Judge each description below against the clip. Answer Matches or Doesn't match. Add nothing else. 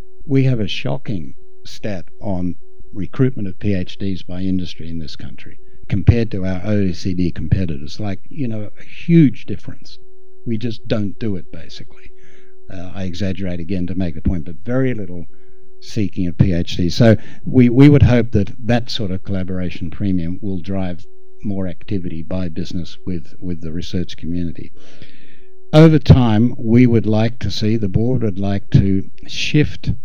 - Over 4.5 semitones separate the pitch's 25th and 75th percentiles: Matches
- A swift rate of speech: Doesn't match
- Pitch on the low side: Matches